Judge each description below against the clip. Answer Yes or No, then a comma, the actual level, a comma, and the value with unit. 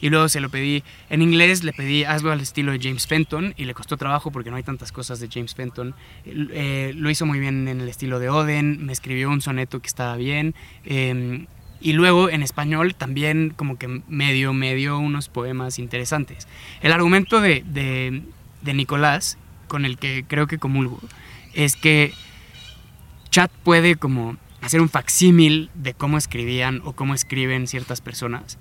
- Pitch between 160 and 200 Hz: No, medium, 140 Hz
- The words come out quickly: No, average, 180 wpm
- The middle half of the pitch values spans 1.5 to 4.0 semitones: Yes, average, 3.1 semitones